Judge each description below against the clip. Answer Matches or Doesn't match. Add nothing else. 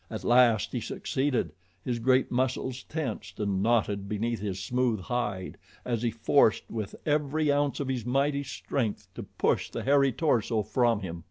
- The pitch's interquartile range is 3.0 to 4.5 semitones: Matches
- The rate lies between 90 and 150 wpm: Doesn't match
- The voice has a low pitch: Matches